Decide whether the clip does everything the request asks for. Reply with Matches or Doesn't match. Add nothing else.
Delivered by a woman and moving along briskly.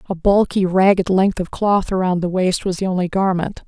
Matches